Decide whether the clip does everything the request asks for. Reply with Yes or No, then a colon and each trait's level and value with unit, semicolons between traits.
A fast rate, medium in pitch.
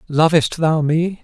No: average, 145 wpm; medium, 160 Hz